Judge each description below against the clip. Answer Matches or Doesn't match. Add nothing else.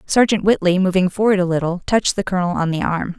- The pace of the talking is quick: Matches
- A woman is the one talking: Matches